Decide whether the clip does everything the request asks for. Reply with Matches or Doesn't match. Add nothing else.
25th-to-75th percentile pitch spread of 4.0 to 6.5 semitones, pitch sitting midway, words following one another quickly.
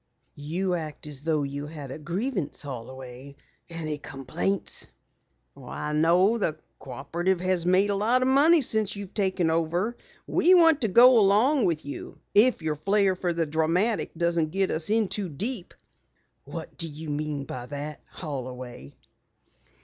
Doesn't match